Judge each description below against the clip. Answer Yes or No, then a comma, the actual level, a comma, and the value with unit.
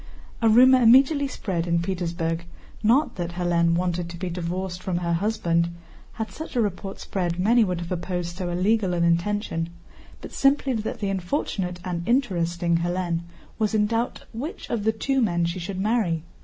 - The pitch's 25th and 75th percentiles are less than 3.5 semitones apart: No, average, 4.4 semitones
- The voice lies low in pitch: No, medium, 185 Hz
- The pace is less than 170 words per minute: No, average, 175 wpm